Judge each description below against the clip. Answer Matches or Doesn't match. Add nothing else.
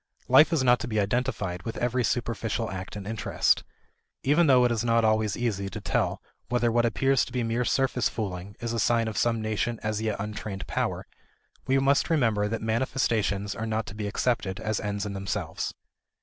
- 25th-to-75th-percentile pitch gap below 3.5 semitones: Matches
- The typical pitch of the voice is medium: Doesn't match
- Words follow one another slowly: Doesn't match